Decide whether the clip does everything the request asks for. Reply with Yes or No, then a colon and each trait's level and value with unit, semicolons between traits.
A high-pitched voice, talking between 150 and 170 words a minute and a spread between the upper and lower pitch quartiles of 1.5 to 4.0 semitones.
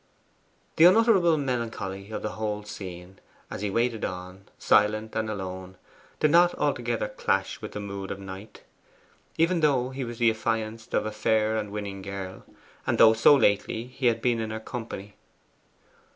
No: low, 110 Hz; average, 165 wpm; average, 3.5 semitones